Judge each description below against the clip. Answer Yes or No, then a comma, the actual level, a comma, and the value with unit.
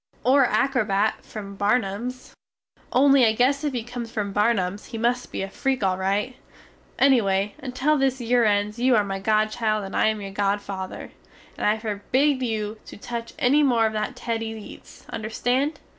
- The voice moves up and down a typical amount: Yes, average, 3.5 semitones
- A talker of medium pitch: No, high, 225 Hz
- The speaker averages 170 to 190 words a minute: Yes, average, 175 wpm